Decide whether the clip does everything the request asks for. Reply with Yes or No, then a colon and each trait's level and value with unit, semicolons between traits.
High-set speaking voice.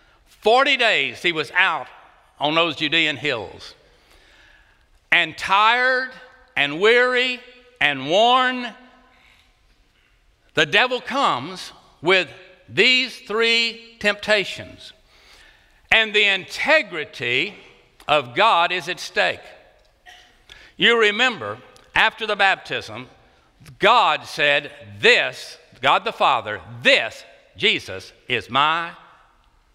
Yes: high, 220 Hz